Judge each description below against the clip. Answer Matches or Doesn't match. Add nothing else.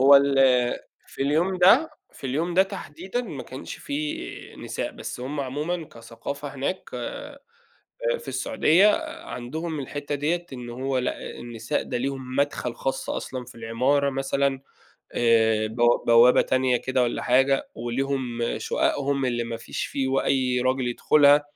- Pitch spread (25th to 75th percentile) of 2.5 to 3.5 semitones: Matches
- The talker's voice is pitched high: Doesn't match